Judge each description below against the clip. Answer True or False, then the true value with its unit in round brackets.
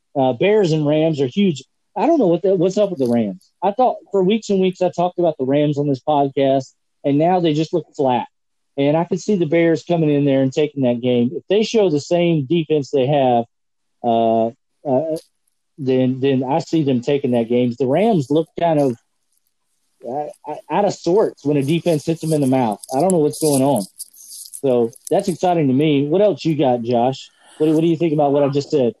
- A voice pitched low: False (150 Hz)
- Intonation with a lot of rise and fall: False (4.3 semitones)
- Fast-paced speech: True (230 wpm)